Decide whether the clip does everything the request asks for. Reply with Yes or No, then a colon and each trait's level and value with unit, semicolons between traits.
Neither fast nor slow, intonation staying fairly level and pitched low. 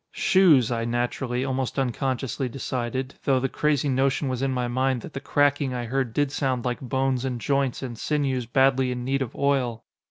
Yes: average, 190 wpm; narrow, 1.8 semitones; low, 130 Hz